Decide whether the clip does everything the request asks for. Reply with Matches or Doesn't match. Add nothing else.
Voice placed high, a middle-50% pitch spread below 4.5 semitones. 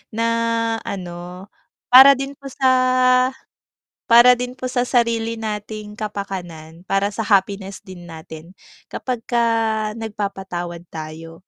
Doesn't match